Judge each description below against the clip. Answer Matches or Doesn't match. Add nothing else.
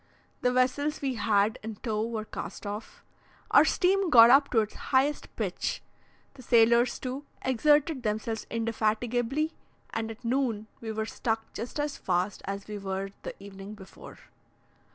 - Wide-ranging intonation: Doesn't match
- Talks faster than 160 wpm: Doesn't match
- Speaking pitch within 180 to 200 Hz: Doesn't match